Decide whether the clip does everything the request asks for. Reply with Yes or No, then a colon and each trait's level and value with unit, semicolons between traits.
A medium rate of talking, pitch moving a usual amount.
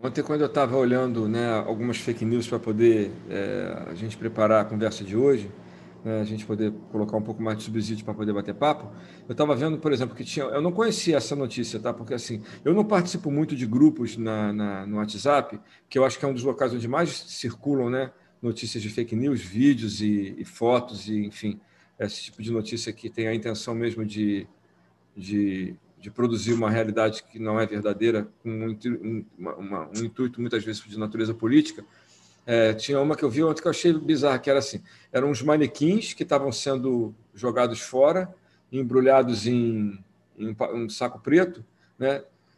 No: fast, 190 wpm; average, 3.8 semitones